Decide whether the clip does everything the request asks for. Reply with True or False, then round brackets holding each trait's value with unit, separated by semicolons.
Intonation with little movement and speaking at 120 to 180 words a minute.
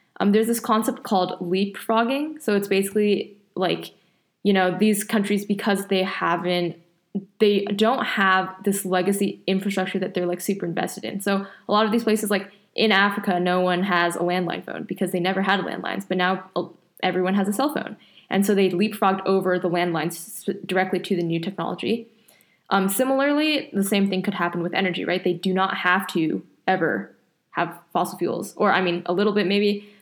False (2.1 semitones; 190 wpm)